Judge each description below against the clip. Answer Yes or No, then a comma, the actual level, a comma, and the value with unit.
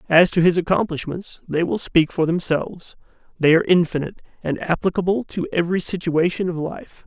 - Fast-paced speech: No, average, 160 wpm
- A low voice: No, medium, 170 Hz